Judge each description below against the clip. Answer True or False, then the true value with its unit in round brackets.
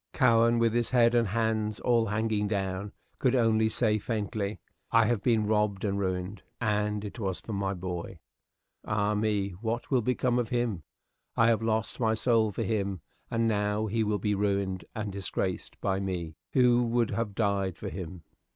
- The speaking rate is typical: True (180 wpm)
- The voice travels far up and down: False (2.6 semitones)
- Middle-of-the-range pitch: False (105 Hz)